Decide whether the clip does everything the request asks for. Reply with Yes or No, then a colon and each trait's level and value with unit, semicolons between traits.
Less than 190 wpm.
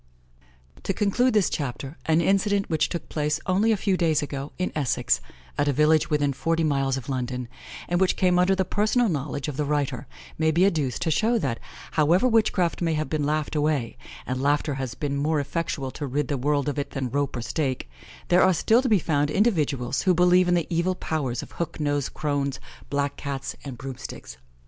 No: fast, 205 wpm